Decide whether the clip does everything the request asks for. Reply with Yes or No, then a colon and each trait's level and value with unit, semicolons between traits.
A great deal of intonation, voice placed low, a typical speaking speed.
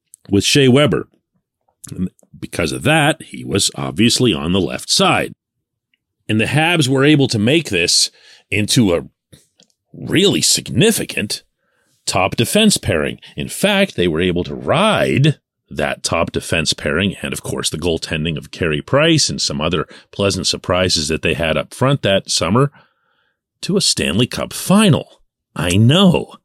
Yes: wide, 8.5 semitones; low, 125 Hz; average, 150 wpm